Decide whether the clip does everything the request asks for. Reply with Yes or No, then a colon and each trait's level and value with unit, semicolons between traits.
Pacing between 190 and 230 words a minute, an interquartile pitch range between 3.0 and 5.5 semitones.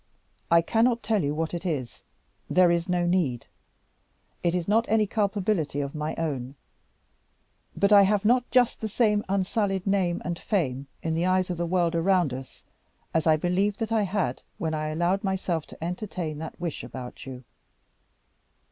No: average, 175 wpm; average, 4.1 semitones